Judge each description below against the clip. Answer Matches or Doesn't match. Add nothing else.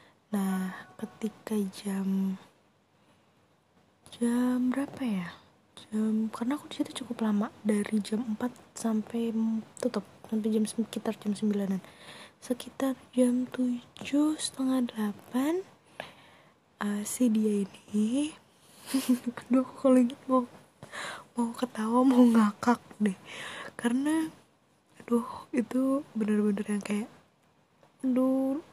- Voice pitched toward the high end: Matches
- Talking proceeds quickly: Doesn't match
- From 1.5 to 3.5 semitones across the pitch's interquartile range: Matches